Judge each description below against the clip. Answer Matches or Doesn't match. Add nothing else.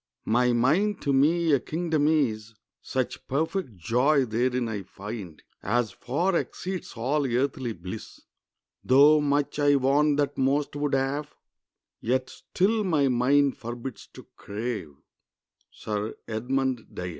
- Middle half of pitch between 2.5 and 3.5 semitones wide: Doesn't match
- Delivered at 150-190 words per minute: Doesn't match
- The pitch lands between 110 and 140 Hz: Matches